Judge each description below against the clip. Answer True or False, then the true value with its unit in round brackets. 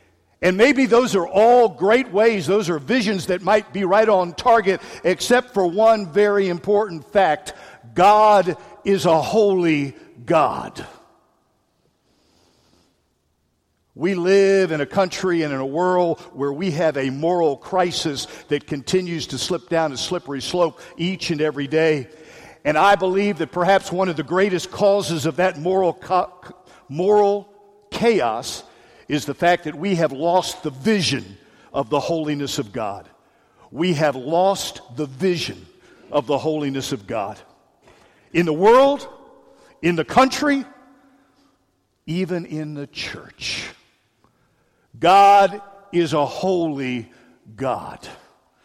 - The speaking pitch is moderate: True (175 Hz)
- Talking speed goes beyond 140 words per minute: False (135 wpm)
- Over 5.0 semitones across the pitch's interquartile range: False (4.7 semitones)